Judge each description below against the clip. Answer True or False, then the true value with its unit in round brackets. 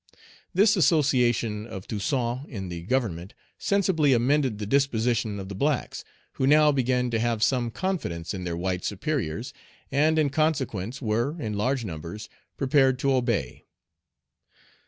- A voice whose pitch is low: True (125 Hz)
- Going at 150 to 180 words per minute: False (140 wpm)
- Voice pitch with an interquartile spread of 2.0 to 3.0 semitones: False (5.2 semitones)